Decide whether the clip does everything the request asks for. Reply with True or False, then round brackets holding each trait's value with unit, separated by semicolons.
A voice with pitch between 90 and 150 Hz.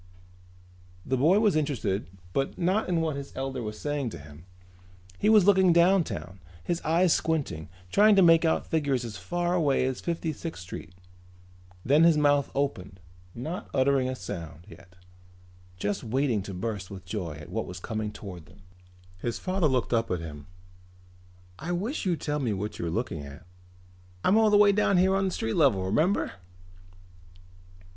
True (135 Hz)